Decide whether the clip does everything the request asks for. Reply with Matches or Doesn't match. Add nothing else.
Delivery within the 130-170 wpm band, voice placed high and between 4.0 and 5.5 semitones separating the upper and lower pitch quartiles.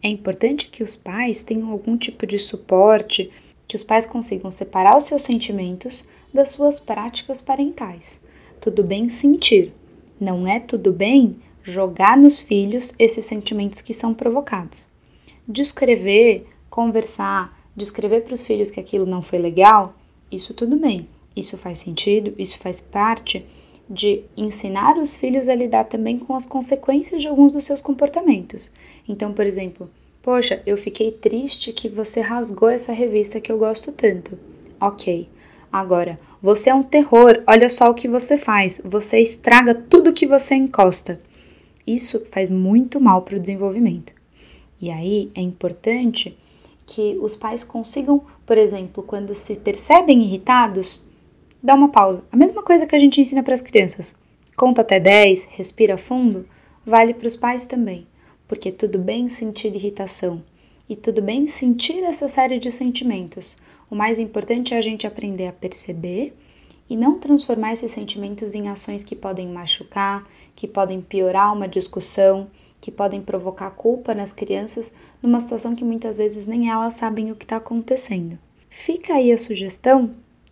Doesn't match